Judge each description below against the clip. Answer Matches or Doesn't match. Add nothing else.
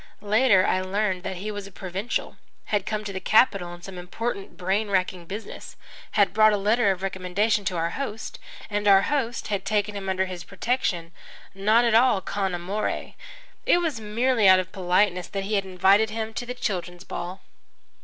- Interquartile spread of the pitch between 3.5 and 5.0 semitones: Doesn't match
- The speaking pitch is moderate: Doesn't match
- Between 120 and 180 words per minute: Doesn't match